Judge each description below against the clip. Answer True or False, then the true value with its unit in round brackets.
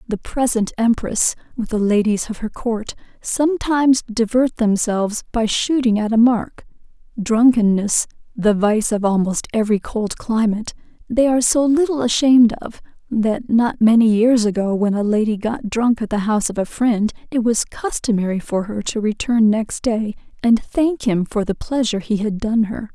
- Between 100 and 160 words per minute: False (175 wpm)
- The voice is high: True (225 Hz)